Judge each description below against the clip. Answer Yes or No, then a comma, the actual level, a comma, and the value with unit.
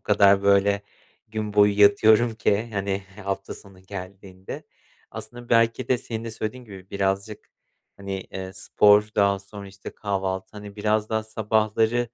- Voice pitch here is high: No, low, 100 Hz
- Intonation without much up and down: Yes, narrow, 1.9 semitones